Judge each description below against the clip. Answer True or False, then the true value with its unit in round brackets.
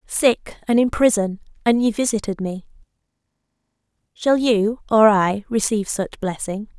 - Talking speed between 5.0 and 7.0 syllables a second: False (4.4 syllables/s)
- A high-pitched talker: True (215 Hz)